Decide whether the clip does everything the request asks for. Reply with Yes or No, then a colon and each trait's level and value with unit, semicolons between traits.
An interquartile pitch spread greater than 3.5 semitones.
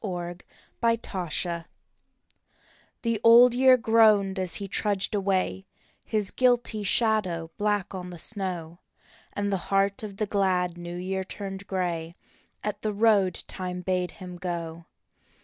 No: average, 2.9 semitones